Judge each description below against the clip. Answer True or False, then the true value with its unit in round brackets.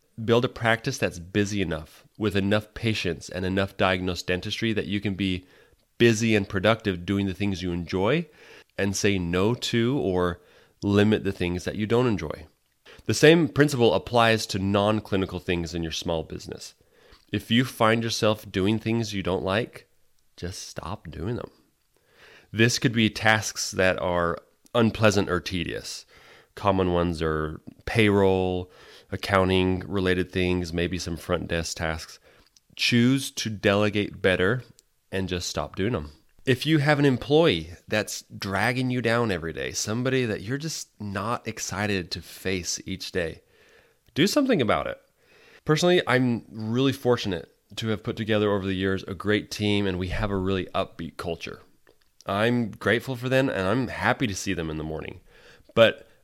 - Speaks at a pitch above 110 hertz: False (100 Hz)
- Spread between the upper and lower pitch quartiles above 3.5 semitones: True (4.1 semitones)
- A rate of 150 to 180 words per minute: True (160 wpm)